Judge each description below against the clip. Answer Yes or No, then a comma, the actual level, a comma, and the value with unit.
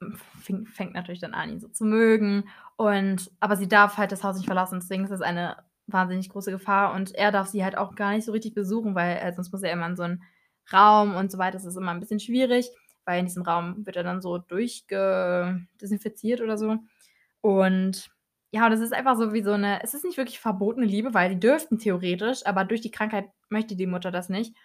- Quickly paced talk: Yes, fast, 230 wpm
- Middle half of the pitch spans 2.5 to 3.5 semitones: Yes, average, 2.9 semitones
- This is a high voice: Yes, high, 200 Hz